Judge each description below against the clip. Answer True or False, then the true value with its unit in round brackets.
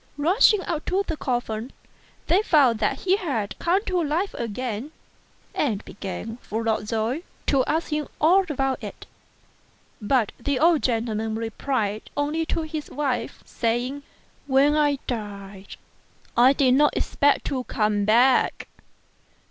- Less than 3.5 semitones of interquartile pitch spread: False (5.2 semitones)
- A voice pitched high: True (265 Hz)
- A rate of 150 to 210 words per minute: False (140 wpm)